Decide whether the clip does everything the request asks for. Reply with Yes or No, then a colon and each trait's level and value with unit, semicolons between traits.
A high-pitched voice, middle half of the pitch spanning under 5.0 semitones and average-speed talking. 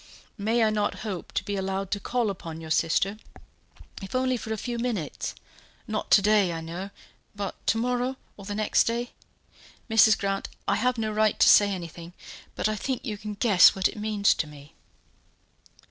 Yes: high, 210 Hz; average, 2.7 semitones; average, 190 wpm